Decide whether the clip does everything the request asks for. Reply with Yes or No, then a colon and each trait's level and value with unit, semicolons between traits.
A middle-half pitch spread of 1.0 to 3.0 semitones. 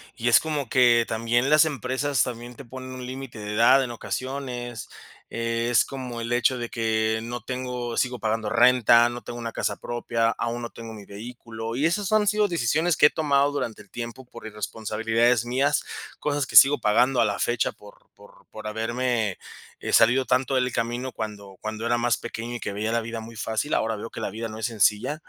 Yes: narrow, 2.4 semitones